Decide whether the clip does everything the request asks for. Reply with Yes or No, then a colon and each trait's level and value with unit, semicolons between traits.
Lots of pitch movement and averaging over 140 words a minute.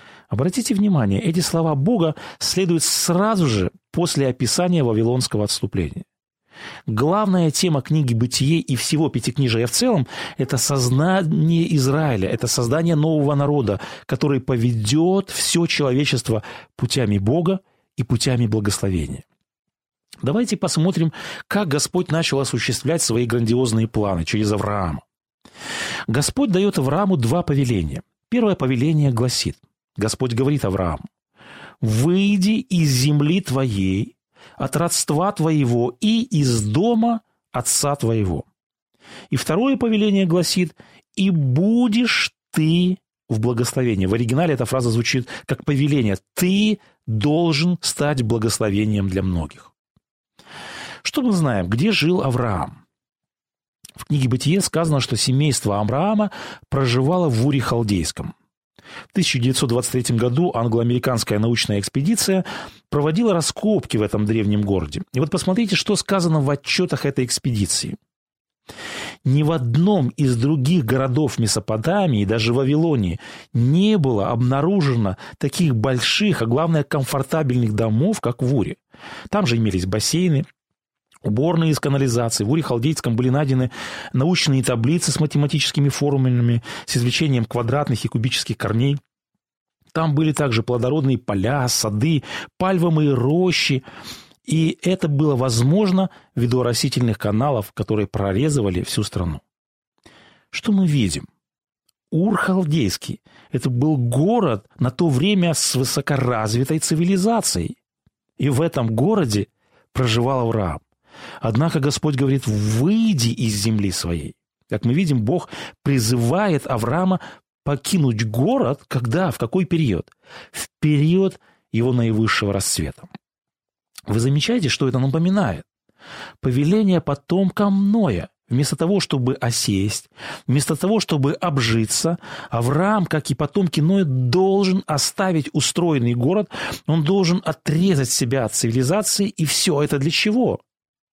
No: wide, 6.1 semitones; average, 115 wpm